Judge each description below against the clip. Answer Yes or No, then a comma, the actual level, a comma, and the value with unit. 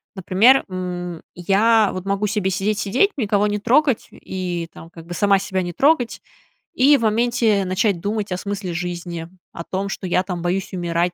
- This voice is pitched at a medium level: No, high, 195 Hz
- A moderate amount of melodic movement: Yes, average, 3.1 semitones